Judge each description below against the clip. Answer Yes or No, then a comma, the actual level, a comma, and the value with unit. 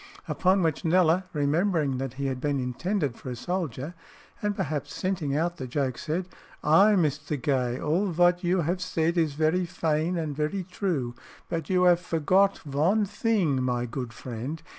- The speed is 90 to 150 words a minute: No, average, 170 wpm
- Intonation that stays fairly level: No, average, 4.5 semitones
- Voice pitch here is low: No, medium, 160 Hz